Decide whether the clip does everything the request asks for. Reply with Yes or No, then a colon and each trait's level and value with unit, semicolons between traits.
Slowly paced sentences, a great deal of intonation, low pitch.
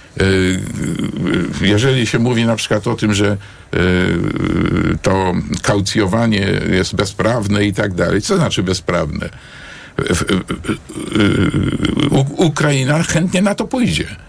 Yes: slow, 95 wpm; wide, 6.0 semitones; low, 105 Hz